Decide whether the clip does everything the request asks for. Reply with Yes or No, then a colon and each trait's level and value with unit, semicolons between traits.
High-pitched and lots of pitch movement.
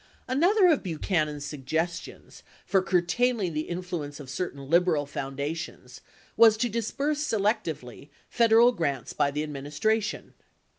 No: medium, 175 Hz; wide, 7.4 semitones